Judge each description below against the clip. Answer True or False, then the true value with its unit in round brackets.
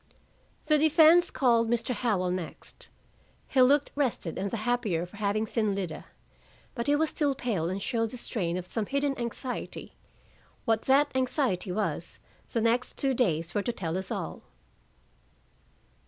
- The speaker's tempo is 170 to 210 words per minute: False (155 wpm)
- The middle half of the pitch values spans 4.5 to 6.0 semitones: True (5.4 semitones)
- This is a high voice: True (230 Hz)